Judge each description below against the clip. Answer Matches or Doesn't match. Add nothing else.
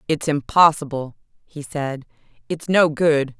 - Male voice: Doesn't match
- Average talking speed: Doesn't match